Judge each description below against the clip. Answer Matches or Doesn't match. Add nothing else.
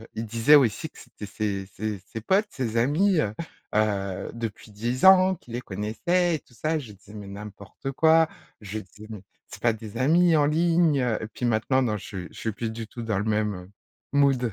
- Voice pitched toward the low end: Matches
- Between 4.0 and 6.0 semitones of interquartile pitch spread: Matches